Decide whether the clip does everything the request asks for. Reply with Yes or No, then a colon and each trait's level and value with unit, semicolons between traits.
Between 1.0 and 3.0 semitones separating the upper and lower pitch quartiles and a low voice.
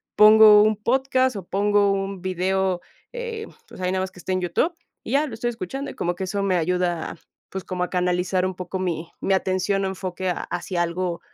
No: narrow, 2.6 semitones; high, 190 Hz